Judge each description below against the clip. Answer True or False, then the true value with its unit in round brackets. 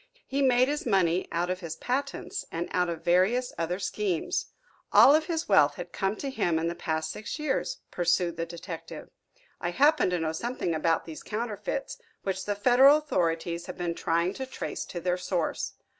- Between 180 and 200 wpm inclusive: True (190 wpm)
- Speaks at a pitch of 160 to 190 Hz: True (185 Hz)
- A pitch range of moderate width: False (6.6 semitones)